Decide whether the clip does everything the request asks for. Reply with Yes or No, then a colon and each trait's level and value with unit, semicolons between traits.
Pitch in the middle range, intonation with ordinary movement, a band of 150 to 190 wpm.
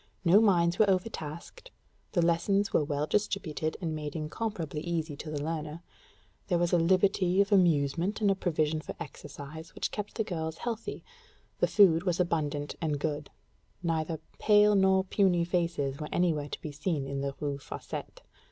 Yes: medium, 170 Hz; average, 4.0 semitones; average, 170 wpm